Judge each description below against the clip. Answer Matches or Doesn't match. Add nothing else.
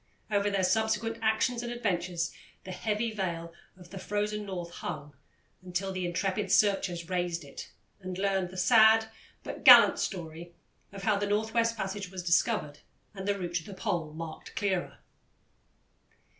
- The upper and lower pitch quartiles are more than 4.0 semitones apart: Doesn't match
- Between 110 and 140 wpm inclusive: Doesn't match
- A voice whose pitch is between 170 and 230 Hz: Matches